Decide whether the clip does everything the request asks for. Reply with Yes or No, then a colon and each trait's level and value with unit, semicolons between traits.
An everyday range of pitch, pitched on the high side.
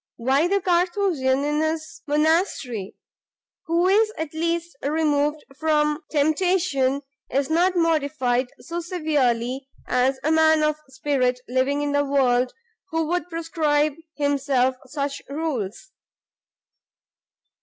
Yes: average, 3.4 semitones; very high, 300 Hz